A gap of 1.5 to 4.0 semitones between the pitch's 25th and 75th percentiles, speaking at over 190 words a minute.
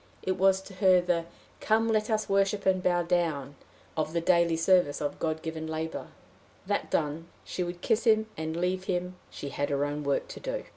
Yes: average, 3.3 semitones; average, 200 wpm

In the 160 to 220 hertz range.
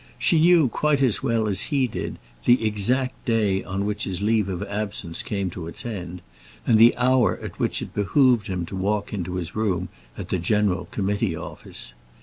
No: low, 105 Hz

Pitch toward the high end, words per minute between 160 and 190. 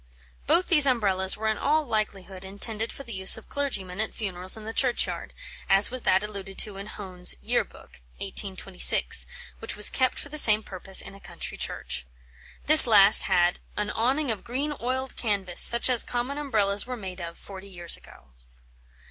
Yes: high, 210 Hz; average, 180 wpm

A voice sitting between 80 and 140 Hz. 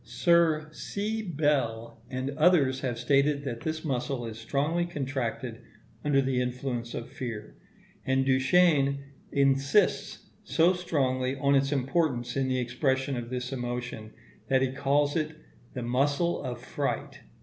Yes: low, 135 Hz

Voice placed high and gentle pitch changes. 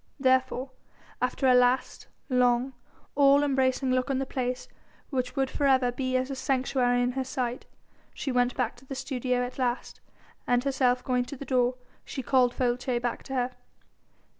Yes: very high, 255 Hz; narrow, 1.3 semitones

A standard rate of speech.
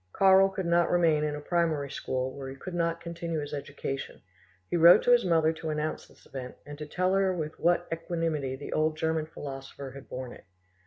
No: fast, 210 wpm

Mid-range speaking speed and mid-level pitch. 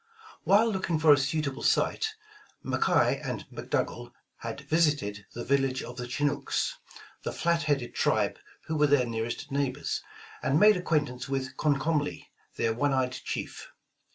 Yes: average, 150 wpm; medium, 145 Hz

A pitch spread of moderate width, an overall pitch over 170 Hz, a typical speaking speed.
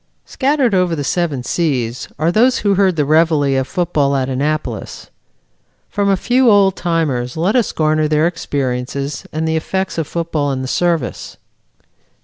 No: average, 4.6 semitones; medium, 160 Hz; average, 160 wpm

